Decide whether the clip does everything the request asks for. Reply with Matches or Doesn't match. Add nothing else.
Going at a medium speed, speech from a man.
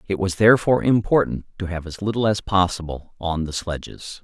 Matches